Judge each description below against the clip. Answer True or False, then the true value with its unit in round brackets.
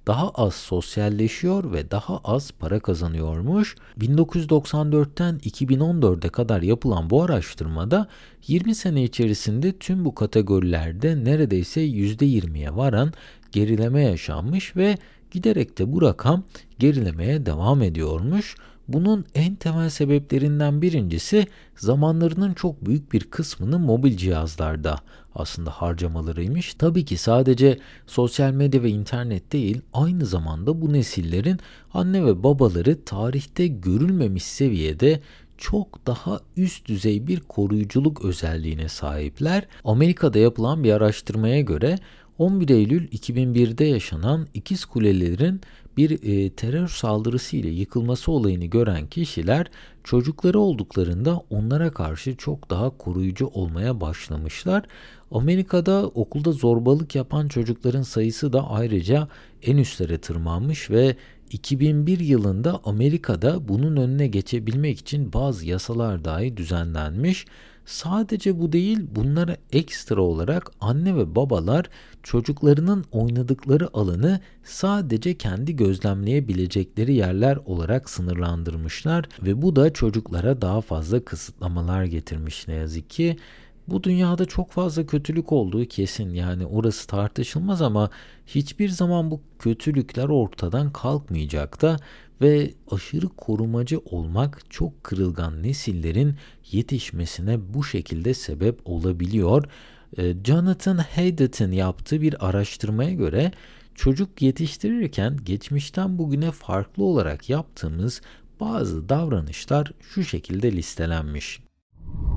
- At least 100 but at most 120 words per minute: True (110 wpm)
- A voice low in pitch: True (125 Hz)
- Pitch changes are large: True (8.0 semitones)